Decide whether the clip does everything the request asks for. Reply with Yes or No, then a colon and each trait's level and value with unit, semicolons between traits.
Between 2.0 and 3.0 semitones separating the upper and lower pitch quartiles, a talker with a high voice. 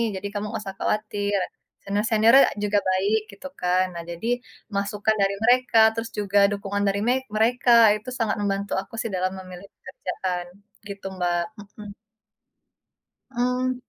Yes: narrow, 2.4 semitones; high, 205 Hz